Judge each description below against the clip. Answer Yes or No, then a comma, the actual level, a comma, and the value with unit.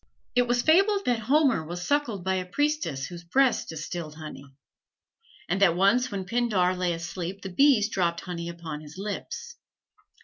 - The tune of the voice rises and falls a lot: Yes, wide, 6.4 semitones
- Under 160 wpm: No, average, 165 wpm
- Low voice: No, high, 190 Hz